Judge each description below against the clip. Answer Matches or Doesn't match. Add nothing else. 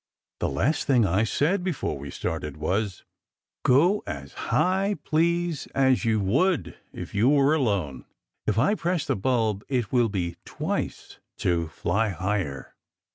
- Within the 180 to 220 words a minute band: Doesn't match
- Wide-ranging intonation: Matches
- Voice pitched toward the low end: Matches